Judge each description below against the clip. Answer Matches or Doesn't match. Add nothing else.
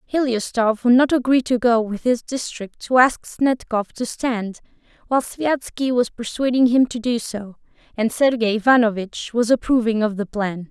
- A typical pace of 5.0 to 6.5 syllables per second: Doesn't match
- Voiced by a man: Doesn't match